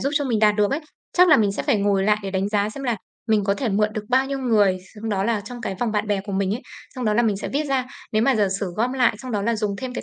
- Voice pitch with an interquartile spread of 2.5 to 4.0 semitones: Yes, average, 3.6 semitones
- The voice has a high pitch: Yes, high, 215 Hz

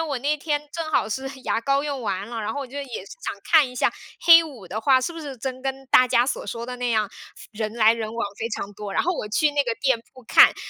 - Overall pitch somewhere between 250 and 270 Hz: Yes, very high, 255 Hz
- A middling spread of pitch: Yes, average, 4.1 semitones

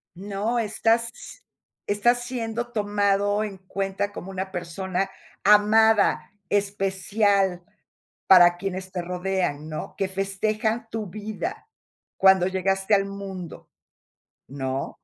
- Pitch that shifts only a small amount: Yes, narrow, 2.1 semitones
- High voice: Yes, high, 195 Hz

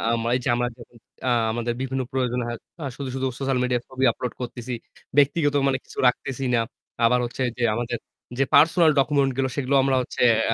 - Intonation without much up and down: Yes, narrow, 1.9 semitones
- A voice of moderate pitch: No, low, 130 Hz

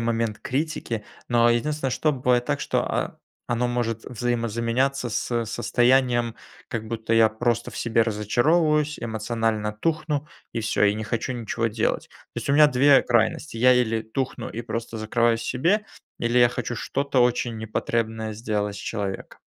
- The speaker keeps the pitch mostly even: Yes, narrow, 2.2 semitones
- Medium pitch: No, low, 120 Hz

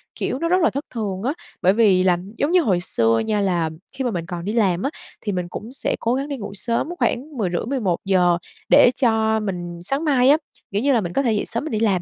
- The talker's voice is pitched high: Yes, high, 215 Hz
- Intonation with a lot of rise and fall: Yes, wide, 6.1 semitones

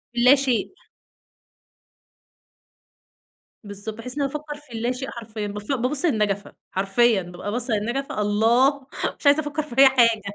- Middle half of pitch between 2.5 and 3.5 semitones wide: No, average, 4.6 semitones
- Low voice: No, high, 240 Hz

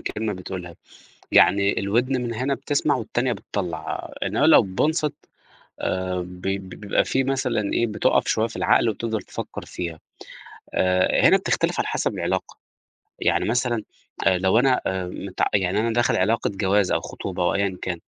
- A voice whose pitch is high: No, low, 100 Hz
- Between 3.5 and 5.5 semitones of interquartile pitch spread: Yes, average, 4.3 semitones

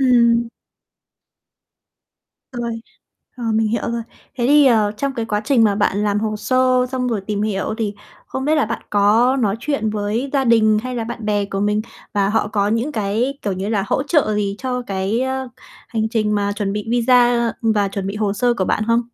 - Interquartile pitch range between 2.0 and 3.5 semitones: Yes, average, 3.1 semitones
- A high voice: Yes, high, 225 Hz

